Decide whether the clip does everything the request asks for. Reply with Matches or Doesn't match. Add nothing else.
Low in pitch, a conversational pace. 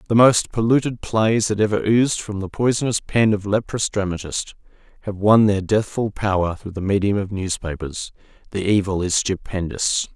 Matches